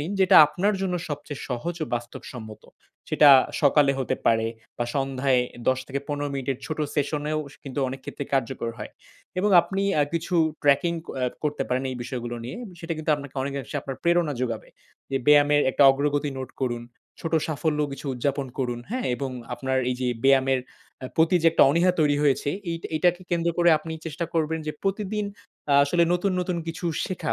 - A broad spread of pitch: No, average, 3.8 semitones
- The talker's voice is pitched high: No, medium, 145 Hz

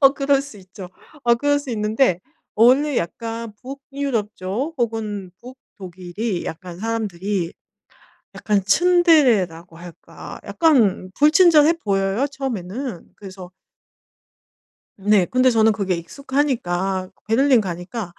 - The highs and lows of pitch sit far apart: Yes, wide, 6.3 semitones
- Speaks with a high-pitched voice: Yes, high, 220 Hz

